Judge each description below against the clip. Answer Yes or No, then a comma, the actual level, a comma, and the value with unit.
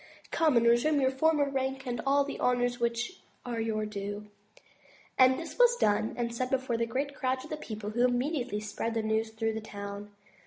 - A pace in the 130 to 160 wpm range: No, average, 190 wpm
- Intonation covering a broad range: No, average, 3.2 semitones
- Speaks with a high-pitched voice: Yes, high, 245 Hz